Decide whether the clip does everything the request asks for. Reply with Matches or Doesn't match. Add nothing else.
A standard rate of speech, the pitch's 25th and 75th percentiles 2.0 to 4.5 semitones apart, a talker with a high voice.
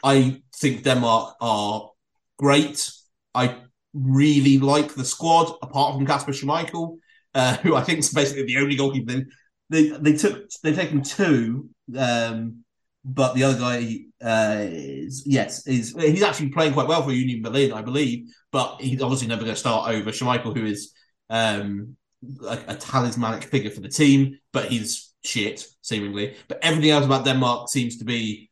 Doesn't match